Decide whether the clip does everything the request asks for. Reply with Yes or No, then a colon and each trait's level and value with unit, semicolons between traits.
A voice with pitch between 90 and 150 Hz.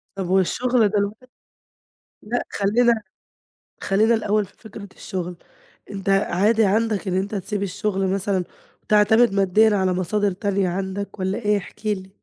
No: high, 200 Hz